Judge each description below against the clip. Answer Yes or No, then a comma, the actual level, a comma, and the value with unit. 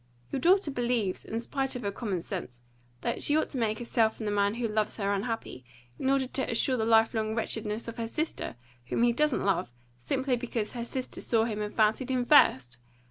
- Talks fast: Yes, fast, 215 wpm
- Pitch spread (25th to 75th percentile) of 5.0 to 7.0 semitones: No, average, 3.3 semitones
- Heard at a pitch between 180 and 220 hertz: No, high, 230 Hz